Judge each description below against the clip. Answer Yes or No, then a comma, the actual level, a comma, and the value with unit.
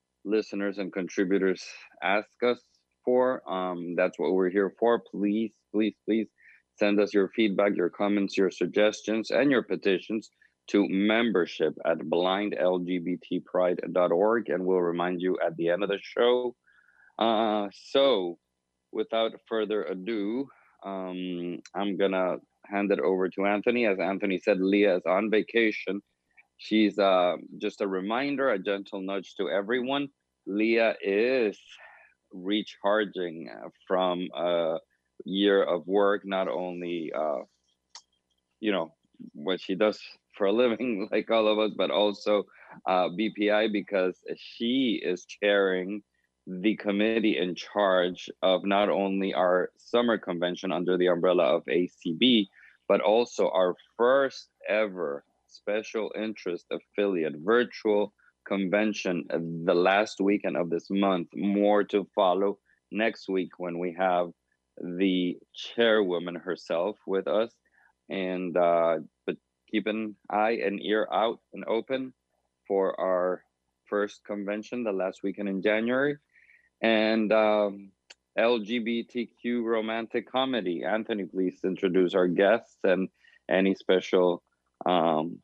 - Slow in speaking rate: Yes, slow, 125 wpm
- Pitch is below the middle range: Yes, low, 100 Hz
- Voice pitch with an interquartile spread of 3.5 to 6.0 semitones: No, average, 2.9 semitones